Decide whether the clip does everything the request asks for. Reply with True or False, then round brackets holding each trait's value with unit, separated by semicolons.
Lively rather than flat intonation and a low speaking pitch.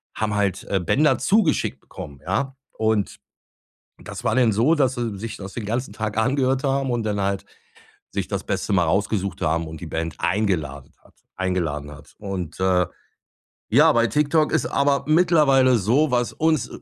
True (6.1 semitones; 110 Hz)